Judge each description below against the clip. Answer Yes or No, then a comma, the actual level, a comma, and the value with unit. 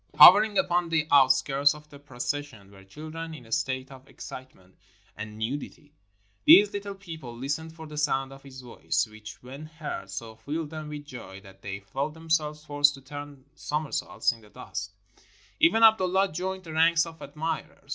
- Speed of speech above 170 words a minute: Yes, average, 185 wpm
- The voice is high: No, medium, 145 Hz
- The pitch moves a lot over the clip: No, average, 4.3 semitones